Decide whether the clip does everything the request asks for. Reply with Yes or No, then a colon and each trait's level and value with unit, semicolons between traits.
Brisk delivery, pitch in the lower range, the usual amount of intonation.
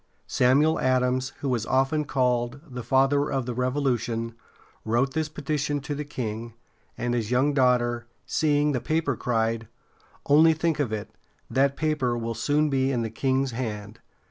No: average, 160 wpm; low, 130 Hz; average, 3.3 semitones